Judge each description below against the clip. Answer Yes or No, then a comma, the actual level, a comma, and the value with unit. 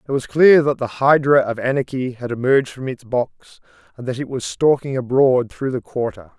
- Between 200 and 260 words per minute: Yes, fast, 205 wpm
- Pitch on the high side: No, low, 130 Hz